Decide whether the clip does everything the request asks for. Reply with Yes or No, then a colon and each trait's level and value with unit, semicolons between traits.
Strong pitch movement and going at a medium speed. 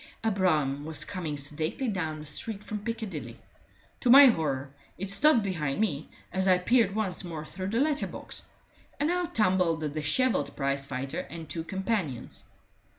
Yes: wide, 6.3 semitones; average, 160 wpm